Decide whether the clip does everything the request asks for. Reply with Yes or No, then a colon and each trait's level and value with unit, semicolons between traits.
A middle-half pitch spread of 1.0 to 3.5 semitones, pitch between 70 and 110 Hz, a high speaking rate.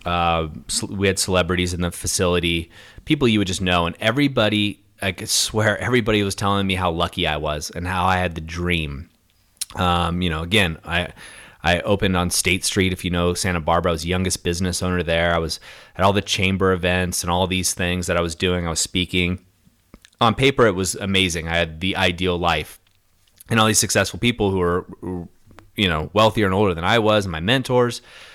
Yes: average, 2.7 semitones; very low, 90 Hz; fast, 210 wpm